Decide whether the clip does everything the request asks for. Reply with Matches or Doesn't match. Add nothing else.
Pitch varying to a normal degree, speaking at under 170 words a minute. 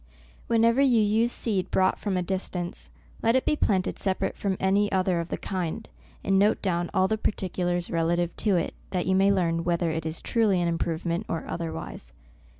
Doesn't match